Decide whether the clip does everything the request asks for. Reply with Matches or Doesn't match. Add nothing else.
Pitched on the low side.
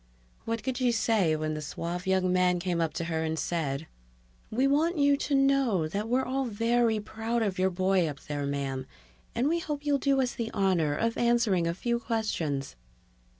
Doesn't match